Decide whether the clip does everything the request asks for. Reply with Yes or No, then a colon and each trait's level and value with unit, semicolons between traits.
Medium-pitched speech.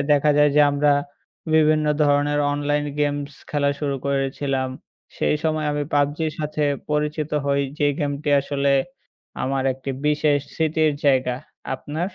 Yes: medium, 145 Hz